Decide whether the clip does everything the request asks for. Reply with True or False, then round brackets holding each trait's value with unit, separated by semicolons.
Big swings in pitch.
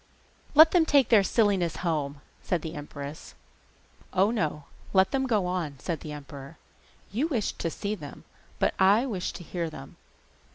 True (6.0 semitones)